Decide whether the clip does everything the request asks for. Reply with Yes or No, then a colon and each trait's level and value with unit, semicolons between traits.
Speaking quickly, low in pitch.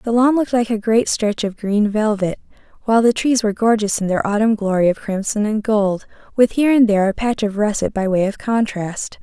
No: fast, 230 wpm; high, 215 Hz